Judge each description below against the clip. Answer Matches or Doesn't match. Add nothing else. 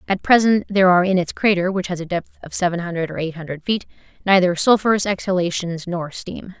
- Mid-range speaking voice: Matches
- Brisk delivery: Matches